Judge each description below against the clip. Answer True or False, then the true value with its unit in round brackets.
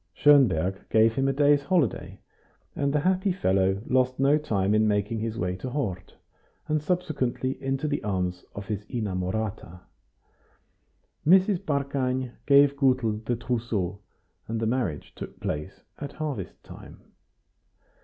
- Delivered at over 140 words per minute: False (135 wpm)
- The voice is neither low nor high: False (125 Hz)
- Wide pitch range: True (5.9 semitones)